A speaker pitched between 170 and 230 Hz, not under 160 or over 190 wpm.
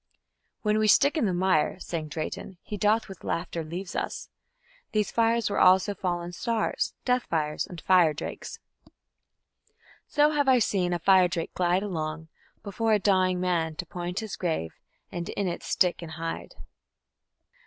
Yes: medium, 185 Hz; average, 165 wpm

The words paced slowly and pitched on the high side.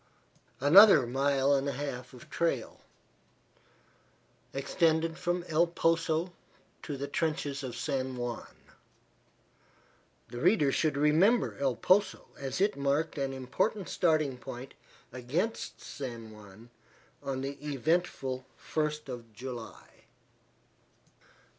No: slow, 110 wpm; medium, 140 Hz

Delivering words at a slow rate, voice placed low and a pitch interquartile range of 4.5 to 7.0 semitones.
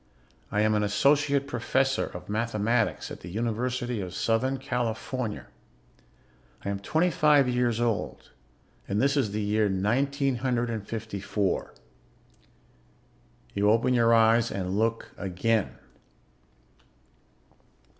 No: slow, 120 wpm; low, 115 Hz; average, 3.4 semitones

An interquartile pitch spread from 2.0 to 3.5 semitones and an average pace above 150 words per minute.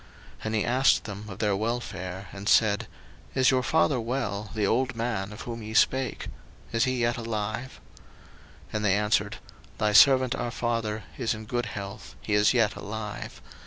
Yes: average, 2.7 semitones; average, 180 wpm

